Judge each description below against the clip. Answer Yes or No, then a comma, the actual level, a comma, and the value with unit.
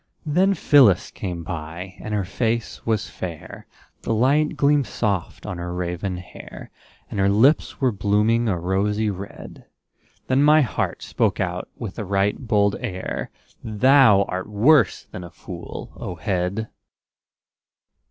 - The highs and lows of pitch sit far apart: No, average, 4.5 semitones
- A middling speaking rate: Yes, average, 145 wpm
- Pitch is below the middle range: Yes, low, 105 Hz